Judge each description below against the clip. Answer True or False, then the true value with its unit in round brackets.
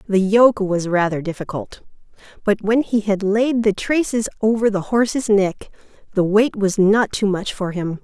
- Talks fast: False (180 wpm)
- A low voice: False (205 Hz)